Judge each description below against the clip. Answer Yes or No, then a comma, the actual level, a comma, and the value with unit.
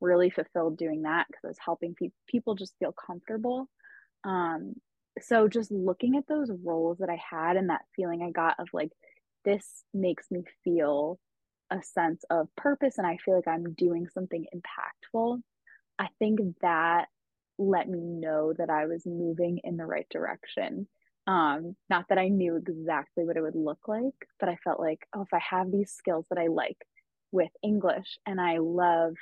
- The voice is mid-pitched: Yes, medium, 180 Hz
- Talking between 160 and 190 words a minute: Yes, average, 185 wpm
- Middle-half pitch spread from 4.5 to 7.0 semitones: No, average, 3.2 semitones